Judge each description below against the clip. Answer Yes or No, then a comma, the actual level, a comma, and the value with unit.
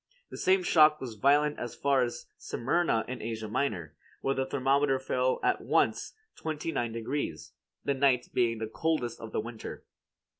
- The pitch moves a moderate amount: Yes, average, 3.9 semitones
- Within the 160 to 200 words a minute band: Yes, average, 165 wpm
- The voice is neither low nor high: No, low, 130 Hz